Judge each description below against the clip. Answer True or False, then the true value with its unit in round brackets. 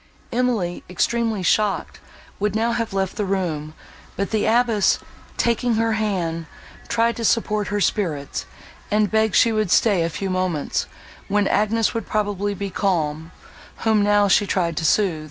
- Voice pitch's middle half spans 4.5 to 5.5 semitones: False (3.2 semitones)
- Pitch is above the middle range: True (205 Hz)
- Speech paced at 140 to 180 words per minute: True (155 wpm)